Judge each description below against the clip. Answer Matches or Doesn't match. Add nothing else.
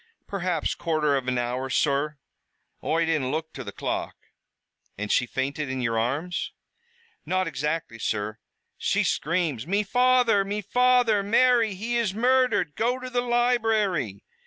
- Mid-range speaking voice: Matches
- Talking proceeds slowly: Doesn't match